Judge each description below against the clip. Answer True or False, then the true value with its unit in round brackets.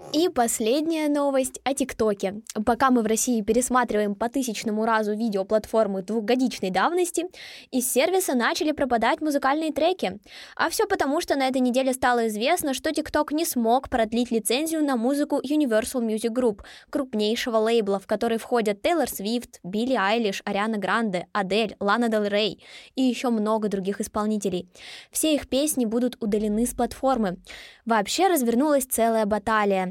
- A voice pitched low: False (240 Hz)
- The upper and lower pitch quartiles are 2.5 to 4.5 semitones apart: True (4.0 semitones)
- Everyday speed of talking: True (145 wpm)